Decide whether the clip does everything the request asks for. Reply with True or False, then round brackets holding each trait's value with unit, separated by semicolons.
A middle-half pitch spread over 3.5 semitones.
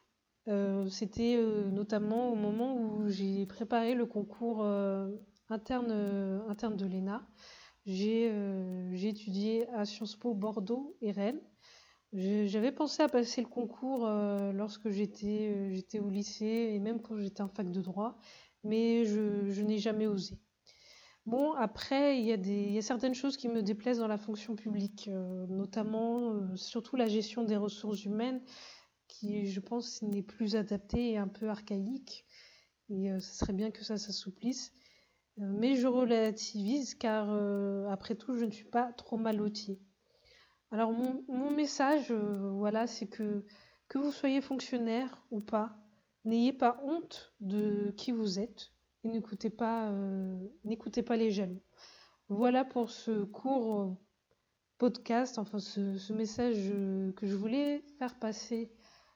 False (2.7 semitones)